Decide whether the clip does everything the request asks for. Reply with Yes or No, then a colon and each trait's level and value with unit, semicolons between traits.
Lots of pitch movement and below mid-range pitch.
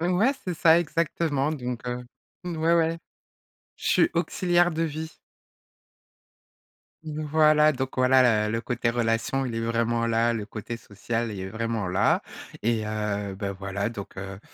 Yes: wide, 6.3 semitones; low, 120 Hz